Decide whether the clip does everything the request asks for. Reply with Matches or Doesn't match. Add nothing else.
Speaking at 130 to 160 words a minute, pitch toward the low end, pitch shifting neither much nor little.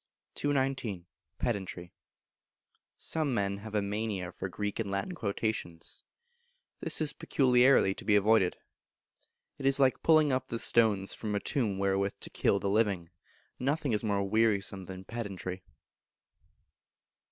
Matches